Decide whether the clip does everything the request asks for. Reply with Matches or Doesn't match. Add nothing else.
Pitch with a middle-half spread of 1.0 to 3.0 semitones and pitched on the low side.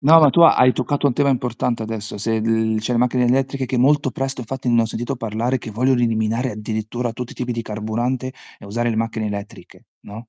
Matches